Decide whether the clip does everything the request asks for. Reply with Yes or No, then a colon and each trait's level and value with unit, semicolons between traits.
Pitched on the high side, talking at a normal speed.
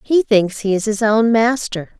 No: high, 220 Hz; fast, 210 wpm